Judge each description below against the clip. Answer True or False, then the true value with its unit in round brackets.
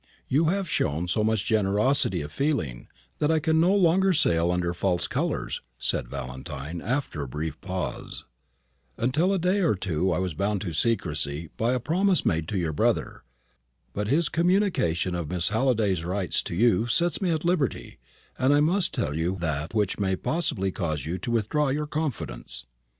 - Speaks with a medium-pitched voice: False (100 Hz)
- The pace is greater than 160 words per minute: True (180 wpm)